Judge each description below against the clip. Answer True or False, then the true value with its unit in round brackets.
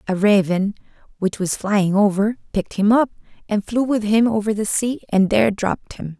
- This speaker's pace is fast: False (195 wpm)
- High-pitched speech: True (210 Hz)